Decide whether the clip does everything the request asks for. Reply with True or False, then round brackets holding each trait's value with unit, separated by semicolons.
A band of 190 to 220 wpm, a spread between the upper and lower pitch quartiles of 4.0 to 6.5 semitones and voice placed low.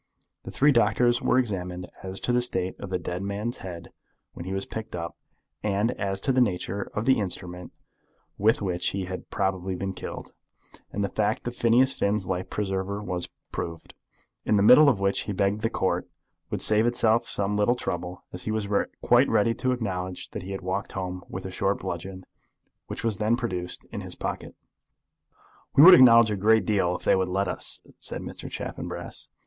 False (200 wpm; 3.3 semitones; 100 Hz)